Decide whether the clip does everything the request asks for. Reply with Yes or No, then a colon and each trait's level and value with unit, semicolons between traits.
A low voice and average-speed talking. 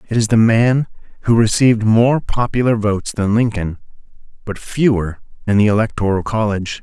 Yes: low, 110 Hz; average, 150 wpm